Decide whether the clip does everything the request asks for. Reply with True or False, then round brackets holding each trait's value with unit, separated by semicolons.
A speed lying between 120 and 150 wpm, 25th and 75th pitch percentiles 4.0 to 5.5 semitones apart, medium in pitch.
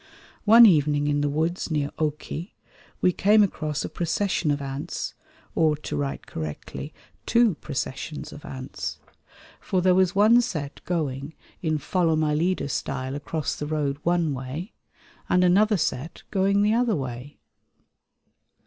True (145 wpm; 4.4 semitones; 155 Hz)